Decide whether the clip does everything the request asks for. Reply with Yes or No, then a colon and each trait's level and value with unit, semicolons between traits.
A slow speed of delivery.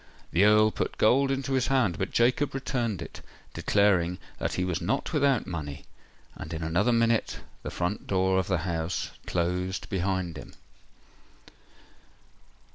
No: average, 145 wpm